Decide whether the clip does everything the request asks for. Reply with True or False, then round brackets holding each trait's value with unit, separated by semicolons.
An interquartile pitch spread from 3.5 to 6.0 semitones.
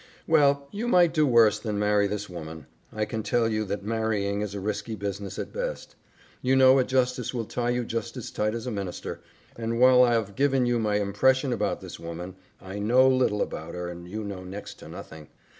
True (3.9 semitones)